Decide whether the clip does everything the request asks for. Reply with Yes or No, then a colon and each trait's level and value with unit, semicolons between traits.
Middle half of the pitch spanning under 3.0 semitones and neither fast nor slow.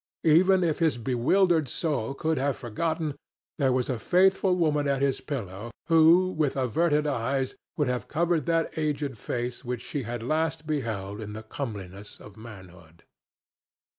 No: wide, 5.5 semitones; average, 155 wpm